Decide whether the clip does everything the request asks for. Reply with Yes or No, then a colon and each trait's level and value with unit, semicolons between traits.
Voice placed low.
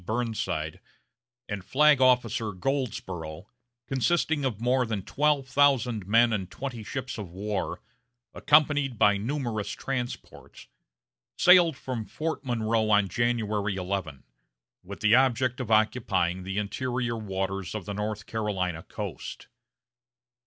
Yes: low, 110 Hz